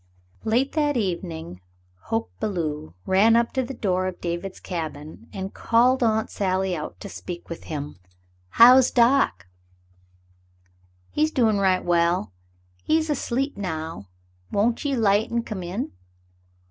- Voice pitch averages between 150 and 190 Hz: No, high, 200 Hz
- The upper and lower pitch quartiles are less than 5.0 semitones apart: No, wide, 5.5 semitones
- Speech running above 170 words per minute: No, slow, 135 wpm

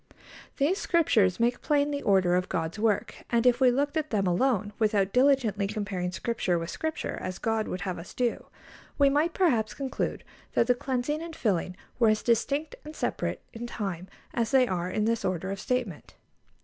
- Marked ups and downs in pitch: Yes, wide, 5.9 semitones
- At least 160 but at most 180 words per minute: No, average, 190 wpm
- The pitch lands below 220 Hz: No, high, 230 Hz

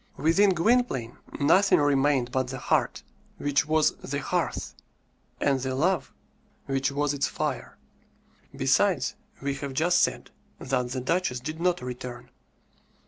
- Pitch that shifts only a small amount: No, average, 4.0 semitones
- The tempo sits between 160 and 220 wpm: No, slow, 135 wpm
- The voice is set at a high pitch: No, medium, 140 Hz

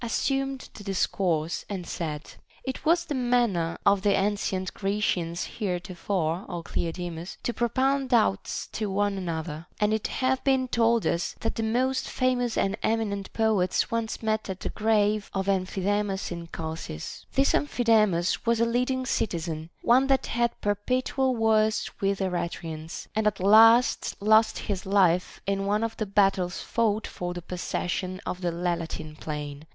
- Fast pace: No, average, 160 wpm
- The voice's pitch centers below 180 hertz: No, high, 205 Hz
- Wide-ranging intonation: No, average, 4.5 semitones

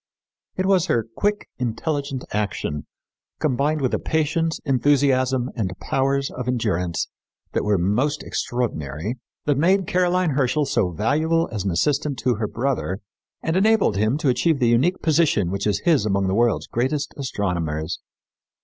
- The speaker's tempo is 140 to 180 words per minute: Yes, average, 155 wpm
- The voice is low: Yes, low, 130 Hz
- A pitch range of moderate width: No, wide, 6.5 semitones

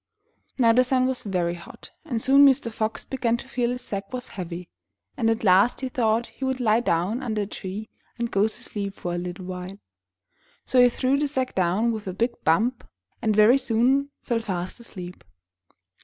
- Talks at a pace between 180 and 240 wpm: Yes, average, 200 wpm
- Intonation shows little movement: No, average, 4.6 semitones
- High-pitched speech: Yes, high, 225 Hz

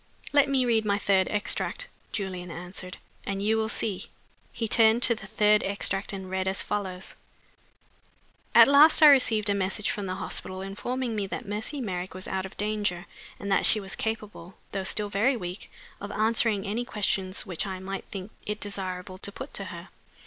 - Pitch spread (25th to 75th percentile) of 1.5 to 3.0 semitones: Yes, narrow, 2.6 semitones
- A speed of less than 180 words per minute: No, average, 185 wpm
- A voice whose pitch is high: Yes, high, 200 Hz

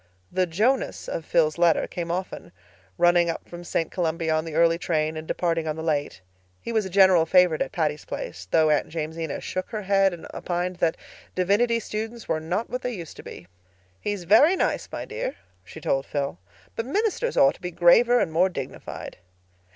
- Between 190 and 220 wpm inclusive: Yes, average, 195 wpm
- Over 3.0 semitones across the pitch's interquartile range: Yes, average, 4.3 semitones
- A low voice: No, medium, 175 Hz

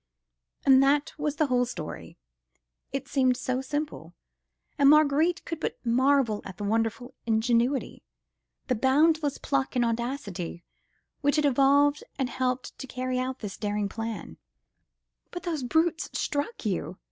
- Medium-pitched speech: No, very high, 260 Hz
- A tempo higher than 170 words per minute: No, average, 140 wpm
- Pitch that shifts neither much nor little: Yes, average, 3.9 semitones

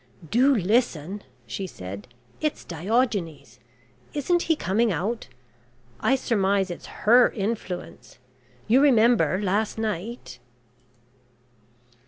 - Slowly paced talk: Yes, slow, 95 wpm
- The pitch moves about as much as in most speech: Yes, average, 4.8 semitones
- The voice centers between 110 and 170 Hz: No, high, 210 Hz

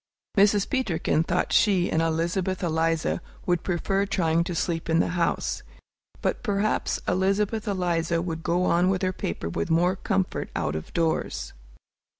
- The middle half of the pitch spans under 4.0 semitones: Yes, average, 2.7 semitones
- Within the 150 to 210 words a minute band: Yes, average, 155 wpm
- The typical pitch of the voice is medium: Yes, medium, 175 Hz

